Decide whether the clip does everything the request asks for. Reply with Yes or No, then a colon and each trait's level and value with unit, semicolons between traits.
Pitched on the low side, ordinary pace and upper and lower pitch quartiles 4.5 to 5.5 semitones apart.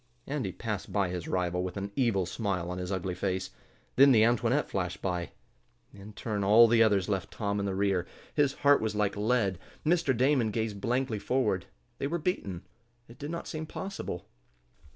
Yes: low, 105 Hz; average, 185 wpm; average, 5.0 semitones